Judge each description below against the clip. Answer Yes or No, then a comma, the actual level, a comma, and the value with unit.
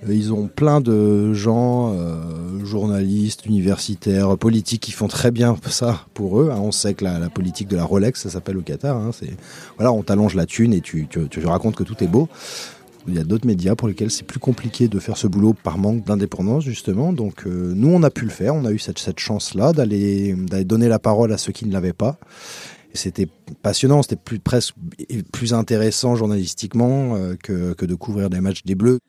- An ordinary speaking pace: No, fast, 225 wpm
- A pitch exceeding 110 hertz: No, low, 105 Hz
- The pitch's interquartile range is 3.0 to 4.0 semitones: Yes, average, 3.3 semitones